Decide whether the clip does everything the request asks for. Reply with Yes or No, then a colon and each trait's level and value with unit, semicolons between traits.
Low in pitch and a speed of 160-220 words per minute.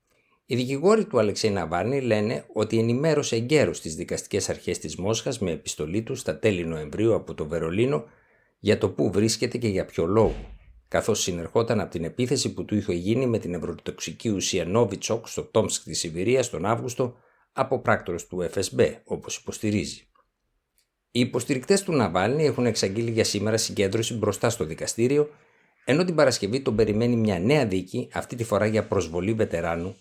Yes: low, 110 Hz; average, 165 wpm